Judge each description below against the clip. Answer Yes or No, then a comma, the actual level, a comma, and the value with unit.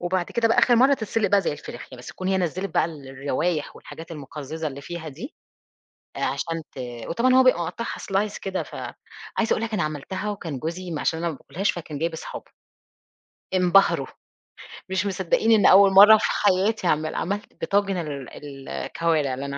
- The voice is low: No, medium, 175 Hz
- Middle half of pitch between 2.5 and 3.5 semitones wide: No, average, 4.5 semitones